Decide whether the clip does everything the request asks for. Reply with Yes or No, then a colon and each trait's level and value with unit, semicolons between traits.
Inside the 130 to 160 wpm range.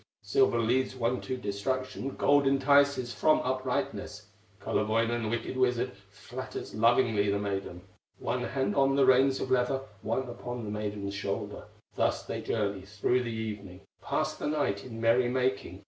Yes: average, 150 wpm